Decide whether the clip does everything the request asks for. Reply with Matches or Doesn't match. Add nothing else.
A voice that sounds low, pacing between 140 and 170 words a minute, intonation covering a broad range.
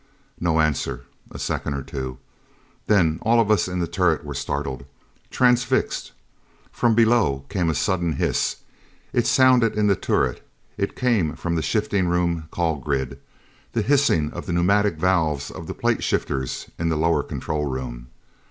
Matches